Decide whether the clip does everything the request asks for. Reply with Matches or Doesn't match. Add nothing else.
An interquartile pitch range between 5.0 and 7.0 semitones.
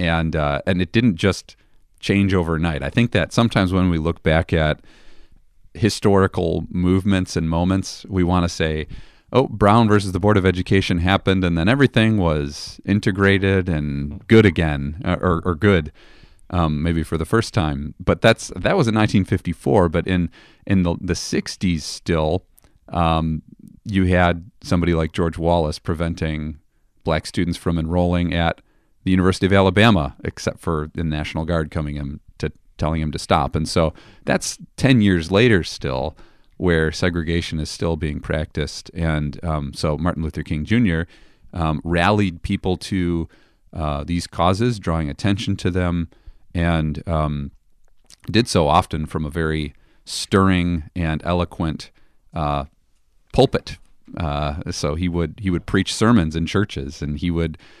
Doesn't match